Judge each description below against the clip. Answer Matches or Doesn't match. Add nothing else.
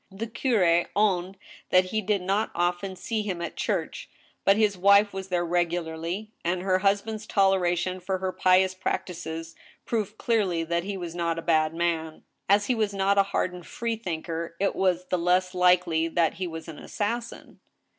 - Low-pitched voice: Doesn't match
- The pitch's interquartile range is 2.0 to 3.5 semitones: Matches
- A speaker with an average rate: Matches